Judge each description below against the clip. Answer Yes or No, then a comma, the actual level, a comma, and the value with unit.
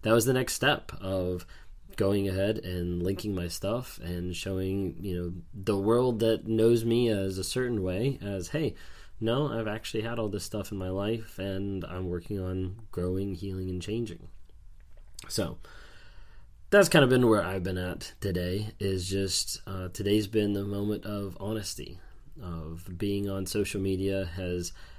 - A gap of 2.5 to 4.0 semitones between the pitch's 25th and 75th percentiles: Yes, average, 2.9 semitones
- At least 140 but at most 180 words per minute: Yes, average, 170 wpm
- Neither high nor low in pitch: No, very low, 95 Hz